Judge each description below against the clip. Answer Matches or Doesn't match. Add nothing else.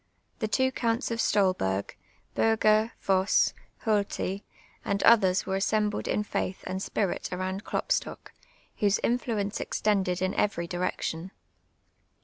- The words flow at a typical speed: Doesn't match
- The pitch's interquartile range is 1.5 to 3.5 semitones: Matches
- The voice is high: Matches